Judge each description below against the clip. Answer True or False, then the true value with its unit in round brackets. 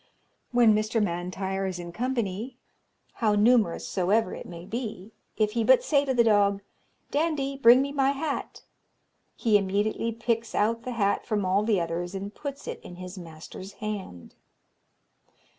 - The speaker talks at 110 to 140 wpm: False (160 wpm)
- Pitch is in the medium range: False (215 Hz)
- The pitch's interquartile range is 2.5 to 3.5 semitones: False (4.0 semitones)